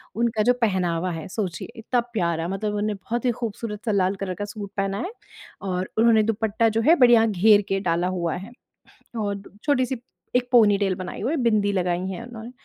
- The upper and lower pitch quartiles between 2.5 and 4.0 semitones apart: Yes, average, 3.4 semitones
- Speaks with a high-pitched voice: Yes, high, 205 Hz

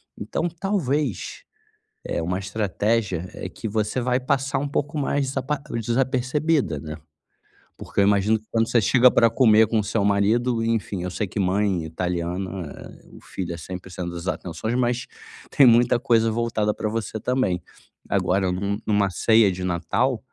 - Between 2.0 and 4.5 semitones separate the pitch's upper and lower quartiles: No, average, 5.1 semitones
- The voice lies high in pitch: No, low, 110 Hz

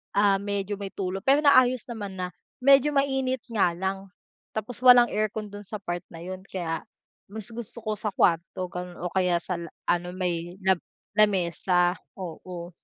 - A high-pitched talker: Yes, high, 195 Hz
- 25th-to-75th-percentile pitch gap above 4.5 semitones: No, average, 3.4 semitones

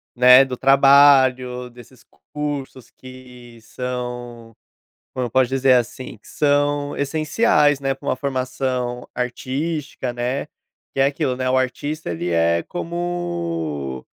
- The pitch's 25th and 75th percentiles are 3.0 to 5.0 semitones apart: No, narrow, 2.6 semitones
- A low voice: Yes, low, 130 Hz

